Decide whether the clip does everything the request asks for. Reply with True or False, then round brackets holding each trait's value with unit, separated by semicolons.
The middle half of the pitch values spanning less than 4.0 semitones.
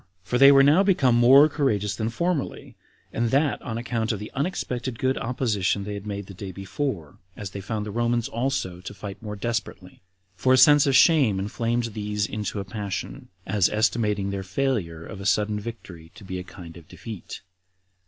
False (4.3 semitones)